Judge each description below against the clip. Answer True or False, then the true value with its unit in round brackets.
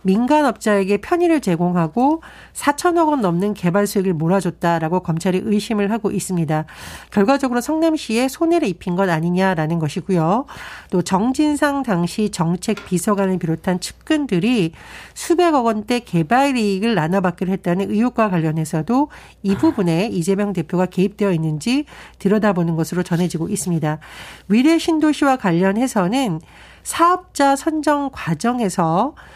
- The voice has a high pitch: True (200 Hz)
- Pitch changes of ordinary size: False (6.9 semitones)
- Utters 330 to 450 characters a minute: True (335 characters per minute)